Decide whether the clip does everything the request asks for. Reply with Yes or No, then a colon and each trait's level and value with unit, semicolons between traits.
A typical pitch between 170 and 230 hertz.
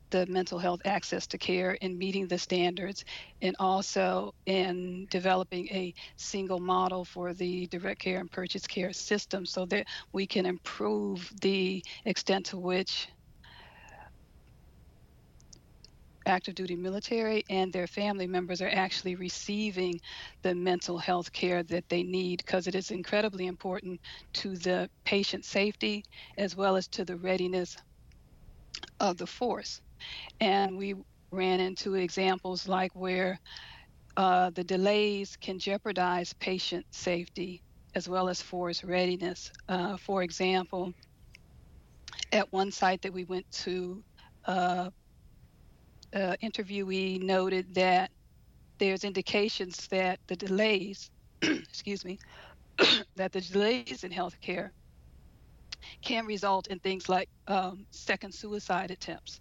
Yes: medium, 185 Hz